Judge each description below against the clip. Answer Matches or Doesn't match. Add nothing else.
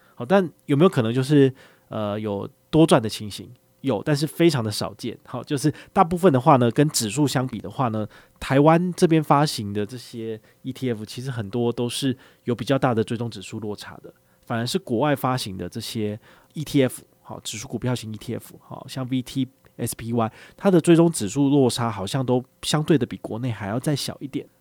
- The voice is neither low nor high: Doesn't match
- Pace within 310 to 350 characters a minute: Doesn't match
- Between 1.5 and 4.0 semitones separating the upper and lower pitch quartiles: Doesn't match